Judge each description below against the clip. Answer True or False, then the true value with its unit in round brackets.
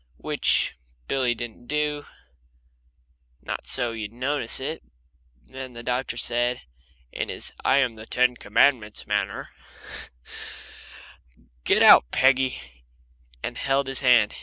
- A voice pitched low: True (125 Hz)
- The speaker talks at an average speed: False (115 wpm)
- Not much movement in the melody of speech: True (2.2 semitones)